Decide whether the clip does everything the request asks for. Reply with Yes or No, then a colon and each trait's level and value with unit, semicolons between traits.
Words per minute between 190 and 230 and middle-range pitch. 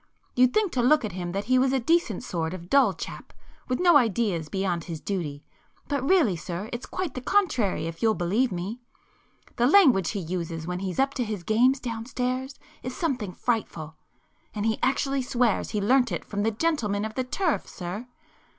No: average, 195 wpm; high, 225 Hz